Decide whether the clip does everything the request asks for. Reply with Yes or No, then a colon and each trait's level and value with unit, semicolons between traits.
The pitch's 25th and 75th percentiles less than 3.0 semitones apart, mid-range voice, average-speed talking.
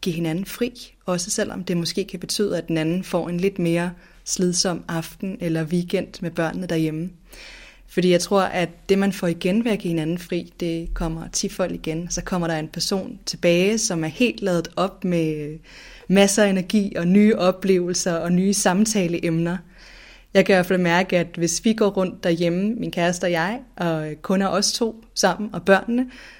Yes: narrow, 2.5 semitones; medium, 180 Hz; average, 195 wpm